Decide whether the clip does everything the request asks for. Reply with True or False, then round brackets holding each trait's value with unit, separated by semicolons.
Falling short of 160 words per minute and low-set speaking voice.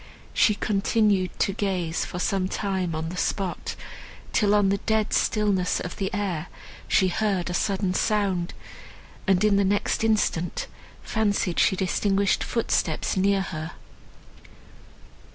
False (135 wpm; 195 Hz)